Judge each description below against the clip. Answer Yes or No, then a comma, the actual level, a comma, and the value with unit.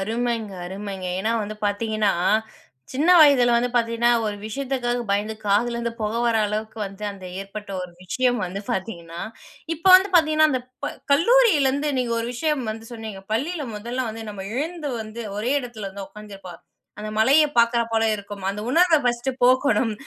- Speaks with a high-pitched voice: Yes, high, 230 Hz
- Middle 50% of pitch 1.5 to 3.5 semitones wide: No, average, 3.9 semitones